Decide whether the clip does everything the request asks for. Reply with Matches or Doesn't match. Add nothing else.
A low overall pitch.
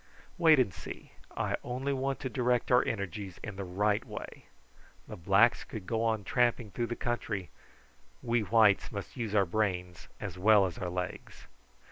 Matches